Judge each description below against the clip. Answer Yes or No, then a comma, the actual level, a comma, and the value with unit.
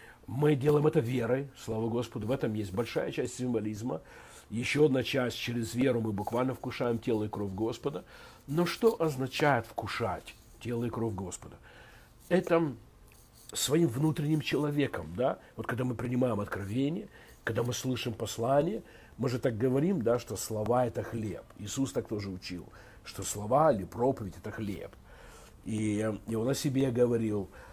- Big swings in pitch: No, average, 3.5 semitones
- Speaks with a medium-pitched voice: No, low, 120 Hz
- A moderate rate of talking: Yes, average, 150 wpm